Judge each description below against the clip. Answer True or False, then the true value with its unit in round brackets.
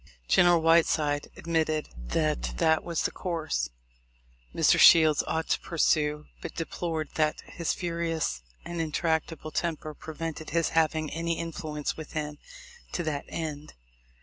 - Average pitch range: False (1.6 semitones)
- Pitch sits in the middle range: True (160 Hz)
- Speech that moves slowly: True (130 wpm)